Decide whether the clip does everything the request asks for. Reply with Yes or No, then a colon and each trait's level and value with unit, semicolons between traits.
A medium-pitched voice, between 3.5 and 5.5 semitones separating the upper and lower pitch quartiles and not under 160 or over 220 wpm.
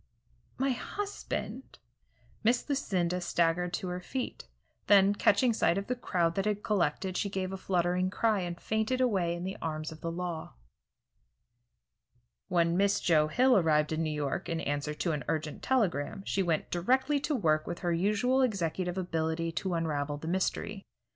Yes: medium, 180 Hz; average, 4.0 semitones; average, 170 wpm